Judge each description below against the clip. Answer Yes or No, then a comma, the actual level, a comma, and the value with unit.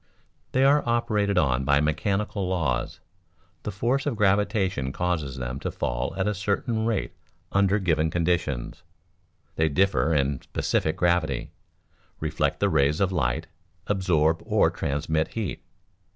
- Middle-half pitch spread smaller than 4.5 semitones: No, wide, 5.6 semitones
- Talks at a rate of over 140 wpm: No, slow, 135 wpm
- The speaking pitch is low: Yes, very low, 90 Hz